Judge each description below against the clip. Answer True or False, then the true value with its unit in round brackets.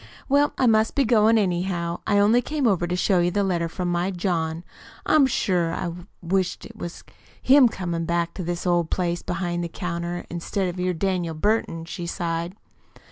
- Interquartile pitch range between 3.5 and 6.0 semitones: False (3.0 semitones)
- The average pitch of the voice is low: False (180 Hz)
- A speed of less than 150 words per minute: False (185 wpm)